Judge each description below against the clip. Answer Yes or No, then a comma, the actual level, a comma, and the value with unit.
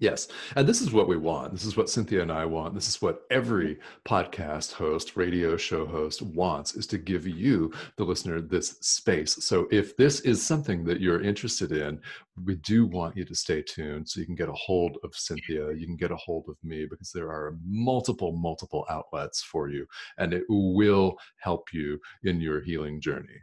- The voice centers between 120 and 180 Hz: No, very low, 85 Hz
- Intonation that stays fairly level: No, average, 3.5 semitones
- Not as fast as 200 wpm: No, fast, 205 wpm